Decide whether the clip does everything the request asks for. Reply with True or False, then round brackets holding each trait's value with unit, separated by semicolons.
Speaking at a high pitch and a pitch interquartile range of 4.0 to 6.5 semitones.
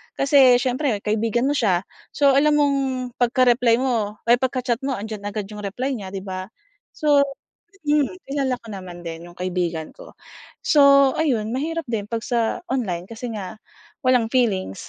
True (240 Hz; 5.0 semitones)